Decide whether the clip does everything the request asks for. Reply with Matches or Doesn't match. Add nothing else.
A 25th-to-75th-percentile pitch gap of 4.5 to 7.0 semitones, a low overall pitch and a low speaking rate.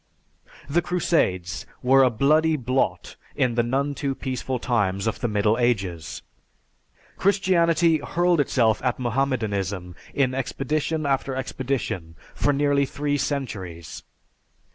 Matches